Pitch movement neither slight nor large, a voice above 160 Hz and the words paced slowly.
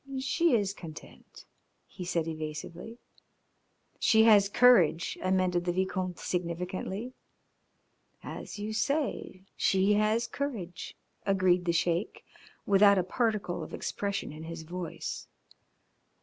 Yes: average, 3.5 semitones; medium, 185 Hz; slow, 110 wpm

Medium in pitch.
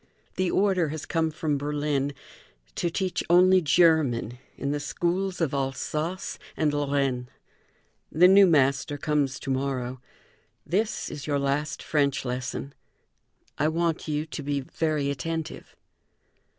Yes: medium, 150 Hz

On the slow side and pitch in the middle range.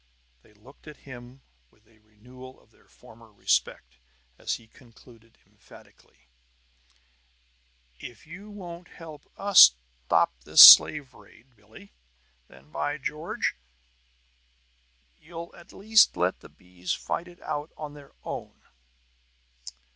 No: slow, 120 wpm; low, 125 Hz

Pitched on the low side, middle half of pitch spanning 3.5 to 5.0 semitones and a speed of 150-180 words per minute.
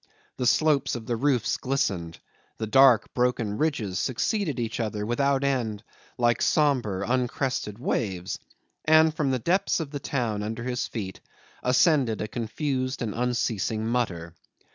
No: low, 125 Hz; average, 4.1 semitones; average, 140 wpm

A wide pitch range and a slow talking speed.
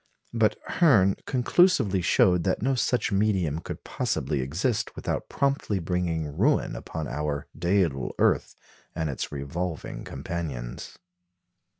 Yes: wide, 6.1 semitones; slow, 115 wpm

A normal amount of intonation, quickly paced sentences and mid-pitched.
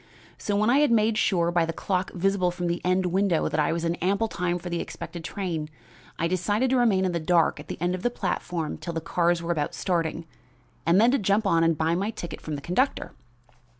Yes: average, 3.0 semitones; fast, 240 wpm; medium, 175 Hz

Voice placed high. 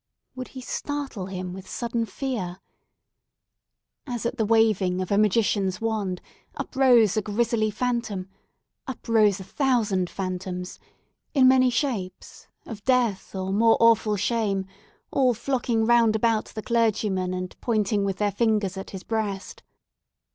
Yes: high, 215 Hz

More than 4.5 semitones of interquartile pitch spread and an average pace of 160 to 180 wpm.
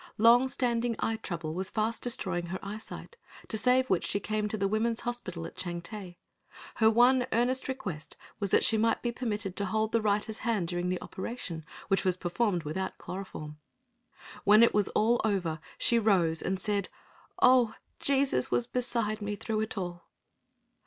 No: average, 4.1 semitones; average, 170 wpm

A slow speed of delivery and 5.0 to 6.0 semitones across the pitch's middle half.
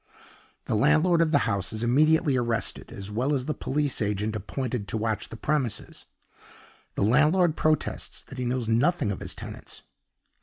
No: average, 165 wpm; wide, 5.5 semitones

